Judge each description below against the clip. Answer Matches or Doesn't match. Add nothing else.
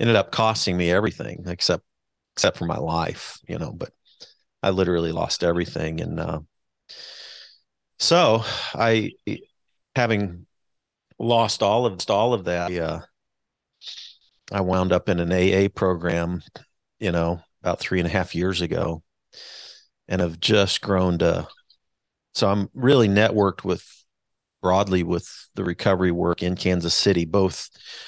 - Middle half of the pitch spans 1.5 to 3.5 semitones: Matches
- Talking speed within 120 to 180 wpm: Matches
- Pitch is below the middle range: Matches